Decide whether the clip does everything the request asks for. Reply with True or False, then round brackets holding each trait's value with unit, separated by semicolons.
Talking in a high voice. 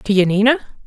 True (210 Hz)